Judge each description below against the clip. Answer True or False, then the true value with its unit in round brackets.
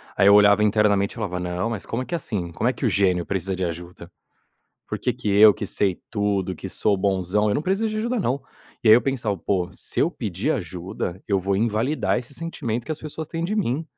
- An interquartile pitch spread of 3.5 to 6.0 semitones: True (5.1 semitones)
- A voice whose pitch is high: False (105 Hz)